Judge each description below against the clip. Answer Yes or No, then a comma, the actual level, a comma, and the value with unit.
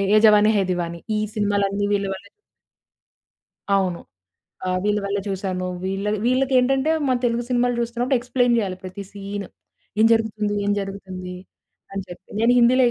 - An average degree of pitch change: Yes, average, 3.6 semitones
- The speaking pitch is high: Yes, high, 205 Hz